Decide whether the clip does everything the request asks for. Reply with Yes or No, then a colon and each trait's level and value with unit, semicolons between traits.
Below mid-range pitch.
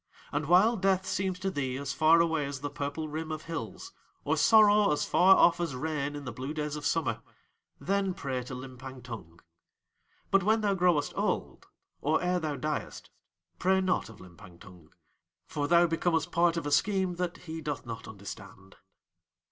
No: medium, 155 Hz